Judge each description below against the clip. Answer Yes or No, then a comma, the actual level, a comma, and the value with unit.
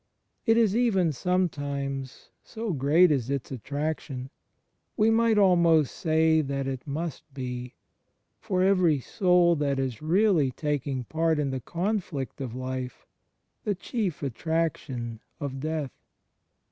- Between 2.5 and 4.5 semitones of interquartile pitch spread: No, average, 5.0 semitones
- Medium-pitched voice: Yes, medium, 150 Hz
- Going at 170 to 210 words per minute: No, slow, 135 wpm